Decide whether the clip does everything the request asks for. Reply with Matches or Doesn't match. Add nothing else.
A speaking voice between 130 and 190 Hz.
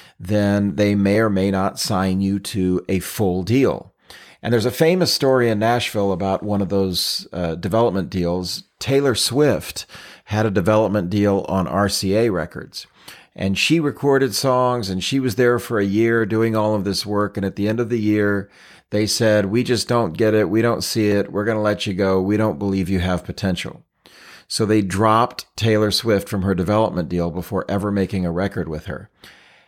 Doesn't match